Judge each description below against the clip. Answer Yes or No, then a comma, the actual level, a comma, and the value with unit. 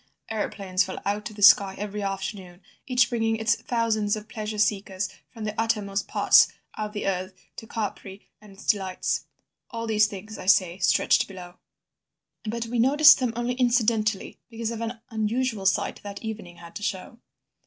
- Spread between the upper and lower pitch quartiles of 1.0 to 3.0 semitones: Yes, narrow, 2.6 semitones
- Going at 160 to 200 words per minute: Yes, average, 170 wpm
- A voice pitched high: Yes, high, 210 Hz